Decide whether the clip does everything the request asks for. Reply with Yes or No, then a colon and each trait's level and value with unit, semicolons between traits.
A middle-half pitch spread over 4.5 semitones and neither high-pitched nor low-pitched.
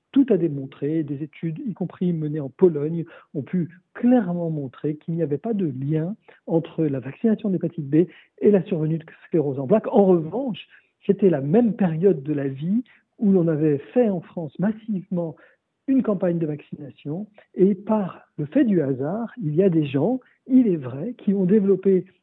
Yes: average, 4.9 semitones; medium, 175 Hz